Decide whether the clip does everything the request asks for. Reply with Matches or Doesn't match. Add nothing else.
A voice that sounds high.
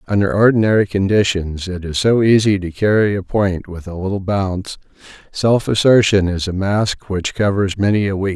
Doesn't match